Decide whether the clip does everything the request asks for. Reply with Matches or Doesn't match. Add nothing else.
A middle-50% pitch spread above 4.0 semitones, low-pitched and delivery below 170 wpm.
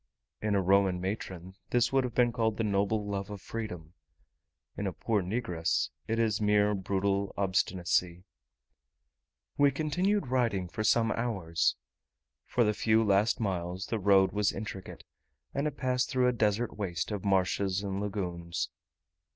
Doesn't match